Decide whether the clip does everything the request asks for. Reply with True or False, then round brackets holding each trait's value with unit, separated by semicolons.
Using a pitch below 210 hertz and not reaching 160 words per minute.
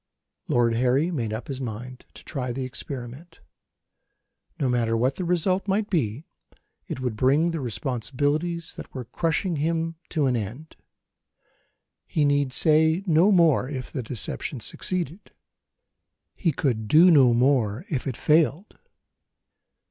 True (140 Hz; 140 wpm)